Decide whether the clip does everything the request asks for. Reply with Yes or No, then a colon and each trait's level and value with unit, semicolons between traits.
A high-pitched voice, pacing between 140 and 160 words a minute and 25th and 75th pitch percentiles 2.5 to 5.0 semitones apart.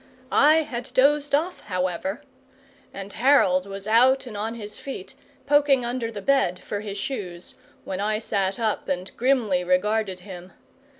No: high, 215 Hz; average, 155 wpm; wide, 5.5 semitones